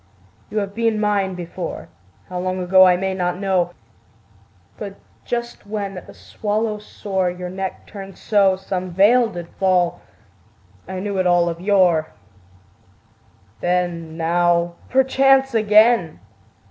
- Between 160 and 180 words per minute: No, slow, 135 wpm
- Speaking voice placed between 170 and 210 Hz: Yes, high, 190 Hz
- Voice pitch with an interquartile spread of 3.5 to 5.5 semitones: No, average, 2.8 semitones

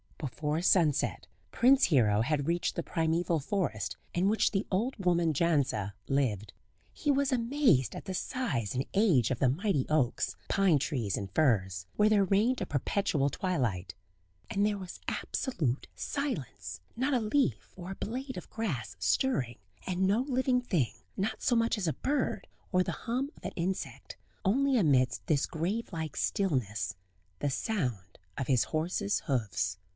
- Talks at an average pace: Yes, average, 160 wpm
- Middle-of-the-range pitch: Yes, medium, 170 Hz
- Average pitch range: No, wide, 8.7 semitones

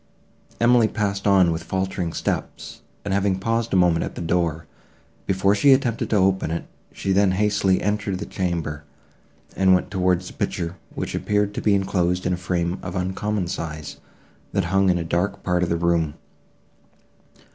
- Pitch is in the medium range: No, very low, 95 Hz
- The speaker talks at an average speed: Yes, average, 175 wpm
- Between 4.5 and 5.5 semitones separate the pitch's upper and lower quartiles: No, average, 2.7 semitones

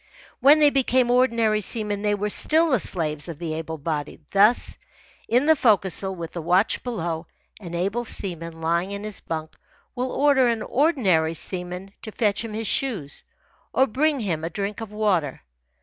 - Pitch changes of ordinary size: No, wide, 6.1 semitones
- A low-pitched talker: No, high, 205 Hz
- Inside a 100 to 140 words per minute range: No, average, 175 wpm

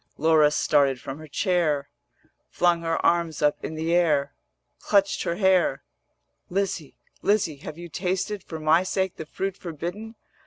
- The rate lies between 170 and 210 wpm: No, average, 150 wpm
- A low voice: No, medium, 170 Hz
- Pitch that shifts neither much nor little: Yes, average, 3.4 semitones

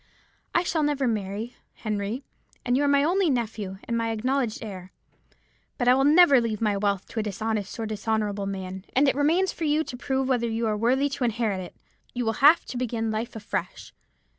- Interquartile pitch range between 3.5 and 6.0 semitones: Yes, average, 4.3 semitones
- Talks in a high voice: Yes, high, 230 Hz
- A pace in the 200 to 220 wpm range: Yes, fast, 205 wpm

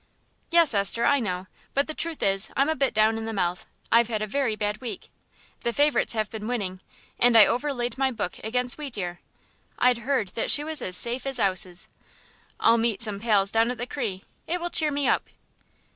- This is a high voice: Yes, high, 235 Hz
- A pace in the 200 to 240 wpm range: Yes, fast, 205 wpm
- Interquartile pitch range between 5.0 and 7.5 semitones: No, average, 4.5 semitones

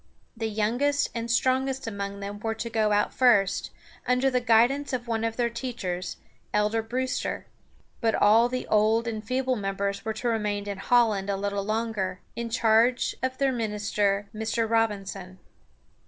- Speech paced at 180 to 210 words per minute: No, average, 165 wpm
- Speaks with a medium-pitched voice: No, high, 225 Hz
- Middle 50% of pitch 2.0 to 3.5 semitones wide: Yes, average, 2.8 semitones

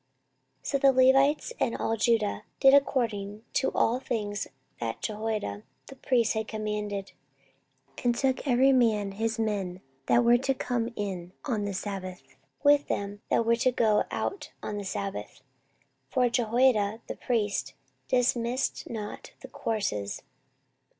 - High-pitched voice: Yes, high, 225 Hz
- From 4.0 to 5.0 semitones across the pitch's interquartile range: No, average, 3.4 semitones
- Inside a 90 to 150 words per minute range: Yes, average, 145 wpm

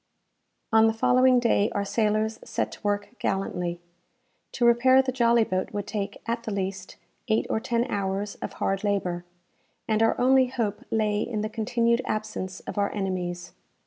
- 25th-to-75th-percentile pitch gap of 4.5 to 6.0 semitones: No, average, 2.9 semitones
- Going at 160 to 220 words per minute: Yes, average, 170 wpm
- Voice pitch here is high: Yes, high, 215 Hz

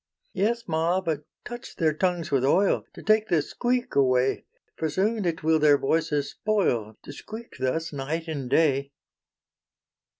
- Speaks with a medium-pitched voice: Yes, medium, 160 Hz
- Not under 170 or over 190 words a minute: No, average, 155 wpm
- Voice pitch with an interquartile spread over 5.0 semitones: Yes, wide, 5.5 semitones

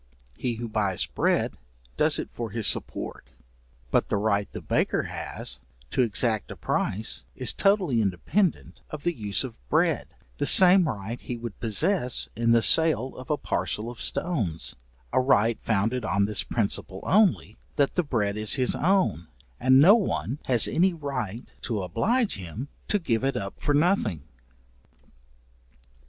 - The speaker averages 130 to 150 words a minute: No, average, 160 wpm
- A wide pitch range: Yes, wide, 6.4 semitones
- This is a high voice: No, low, 120 Hz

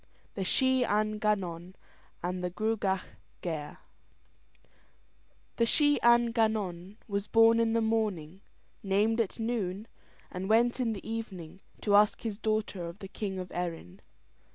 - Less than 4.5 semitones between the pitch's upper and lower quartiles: Yes, average, 3.5 semitones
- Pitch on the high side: Yes, high, 210 Hz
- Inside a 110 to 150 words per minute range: Yes, average, 140 wpm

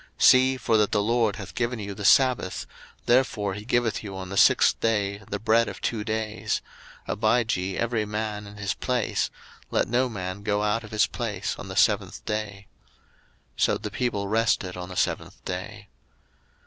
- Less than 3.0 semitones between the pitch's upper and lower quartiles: Yes, narrow, 2.5 semitones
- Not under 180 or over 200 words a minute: Yes, average, 185 wpm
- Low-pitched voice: Yes, low, 105 Hz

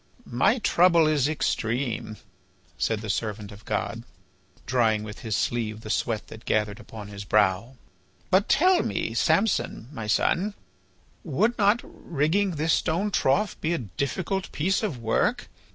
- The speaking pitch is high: No, low, 130 Hz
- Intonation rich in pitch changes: Yes, wide, 8.8 semitones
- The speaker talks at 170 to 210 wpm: No, average, 145 wpm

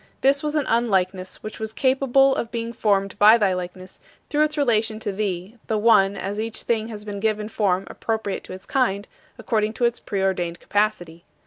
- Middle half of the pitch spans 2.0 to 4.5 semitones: Yes, average, 3.2 semitones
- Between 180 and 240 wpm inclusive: Yes, average, 190 wpm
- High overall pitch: Yes, high, 215 Hz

